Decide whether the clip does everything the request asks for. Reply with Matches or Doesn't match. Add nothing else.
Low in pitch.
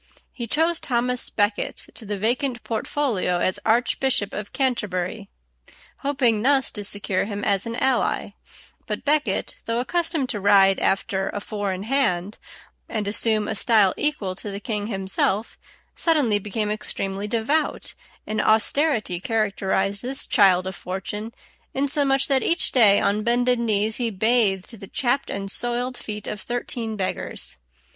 Doesn't match